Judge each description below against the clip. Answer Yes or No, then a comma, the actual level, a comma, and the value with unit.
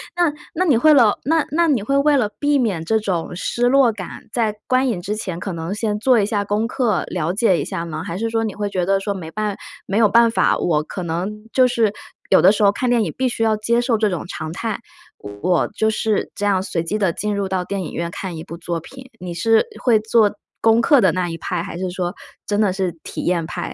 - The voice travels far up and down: No, average, 4.2 semitones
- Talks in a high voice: Yes, high, 210 Hz